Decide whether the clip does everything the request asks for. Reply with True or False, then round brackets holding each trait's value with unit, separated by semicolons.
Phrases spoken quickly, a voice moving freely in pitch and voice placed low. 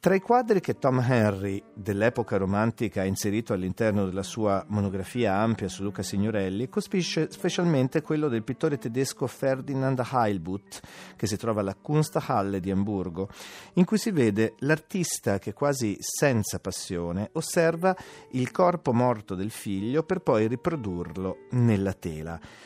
False (140 wpm; 6.7 semitones; 115 Hz)